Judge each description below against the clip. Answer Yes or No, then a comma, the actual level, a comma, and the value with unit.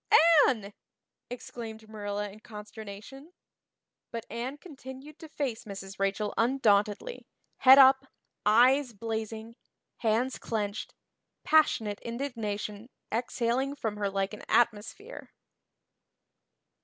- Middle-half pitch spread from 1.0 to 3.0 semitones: No, average, 4.0 semitones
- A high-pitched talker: Yes, high, 225 Hz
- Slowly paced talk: Yes, slow, 95 wpm